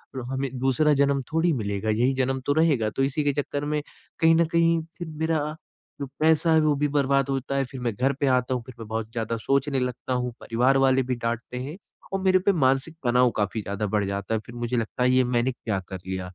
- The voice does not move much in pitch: No, average, 3.6 semitones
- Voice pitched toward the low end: Yes, low, 130 Hz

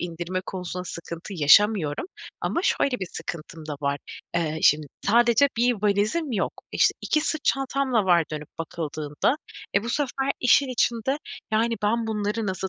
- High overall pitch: Yes, high, 205 Hz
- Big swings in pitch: Yes, wide, 6.4 semitones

